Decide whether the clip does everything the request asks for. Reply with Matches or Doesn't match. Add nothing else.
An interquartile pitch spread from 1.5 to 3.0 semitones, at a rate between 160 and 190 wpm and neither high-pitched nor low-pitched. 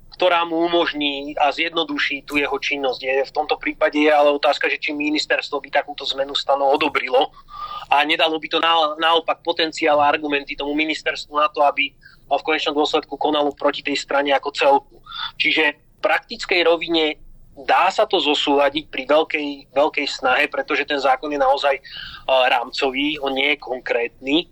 Matches